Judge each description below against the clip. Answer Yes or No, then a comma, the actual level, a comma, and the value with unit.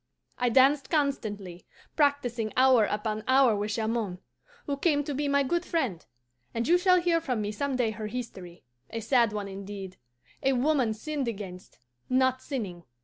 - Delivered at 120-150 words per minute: No, average, 165 wpm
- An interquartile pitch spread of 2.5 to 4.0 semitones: No, average, 5.0 semitones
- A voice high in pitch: Yes, high, 245 Hz